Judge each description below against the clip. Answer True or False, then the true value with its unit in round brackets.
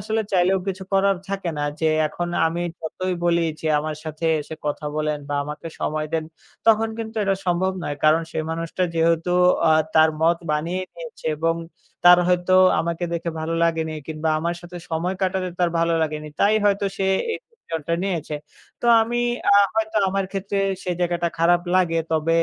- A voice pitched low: False (170 Hz)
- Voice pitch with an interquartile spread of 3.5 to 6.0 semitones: False (2.9 semitones)